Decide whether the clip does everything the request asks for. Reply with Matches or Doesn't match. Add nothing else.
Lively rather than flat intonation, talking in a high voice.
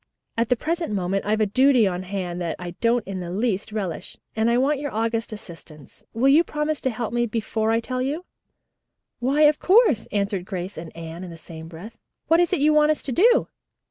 Matches